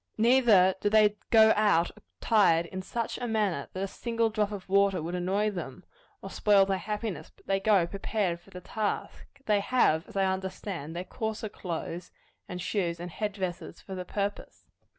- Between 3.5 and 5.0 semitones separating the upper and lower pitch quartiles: No, average, 2.9 semitones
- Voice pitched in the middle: No, high, 195 Hz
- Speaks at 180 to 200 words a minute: Yes, average, 185 wpm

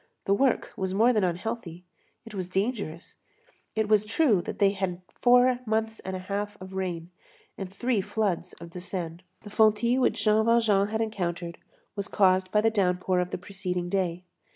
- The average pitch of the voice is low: No, high, 195 Hz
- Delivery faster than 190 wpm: No, average, 180 wpm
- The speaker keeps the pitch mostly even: No, average, 3.2 semitones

